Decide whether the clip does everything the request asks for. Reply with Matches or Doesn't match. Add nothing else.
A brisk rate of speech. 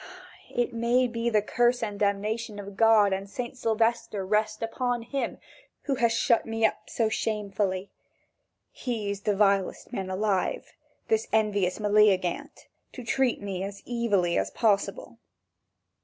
Doesn't match